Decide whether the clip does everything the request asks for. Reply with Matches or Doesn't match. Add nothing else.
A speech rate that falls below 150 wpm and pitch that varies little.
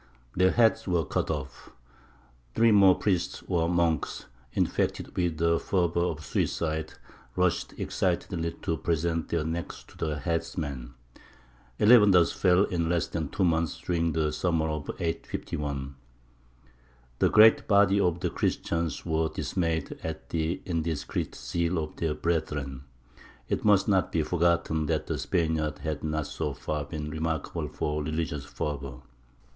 Matches